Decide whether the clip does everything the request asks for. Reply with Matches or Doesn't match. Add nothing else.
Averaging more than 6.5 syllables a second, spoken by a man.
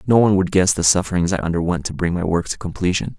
Matches